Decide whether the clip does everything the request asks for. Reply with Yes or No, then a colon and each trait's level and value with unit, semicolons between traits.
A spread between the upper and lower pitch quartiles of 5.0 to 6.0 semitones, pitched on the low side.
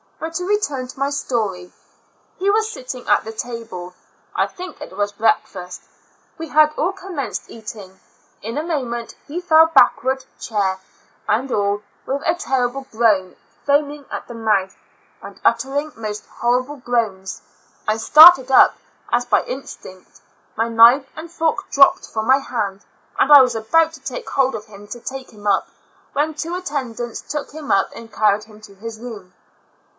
No: wide, 5.4 semitones; high, 245 Hz